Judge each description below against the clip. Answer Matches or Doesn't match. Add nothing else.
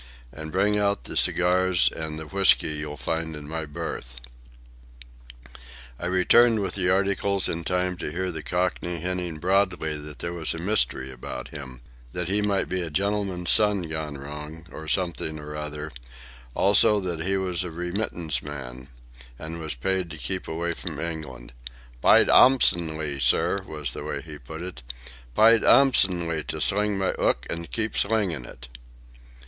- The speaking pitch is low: Matches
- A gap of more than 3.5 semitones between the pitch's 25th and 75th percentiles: Matches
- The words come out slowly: Doesn't match